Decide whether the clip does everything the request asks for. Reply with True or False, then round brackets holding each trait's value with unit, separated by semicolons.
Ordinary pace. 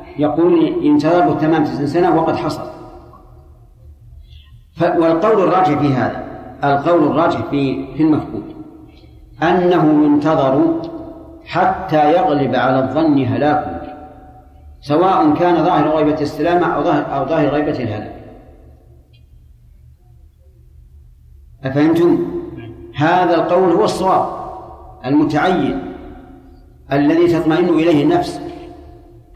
True (90 wpm)